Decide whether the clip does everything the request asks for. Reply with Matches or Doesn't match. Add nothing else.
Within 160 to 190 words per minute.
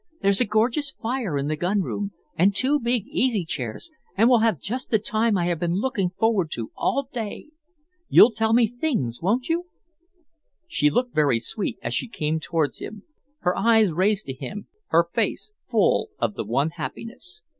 Matches